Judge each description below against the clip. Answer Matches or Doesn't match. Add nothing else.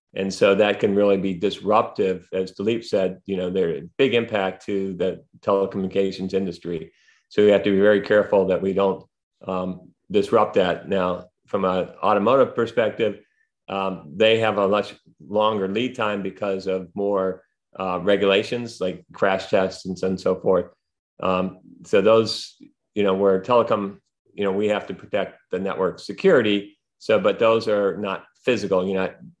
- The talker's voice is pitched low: Matches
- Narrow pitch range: Matches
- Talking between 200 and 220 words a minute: Doesn't match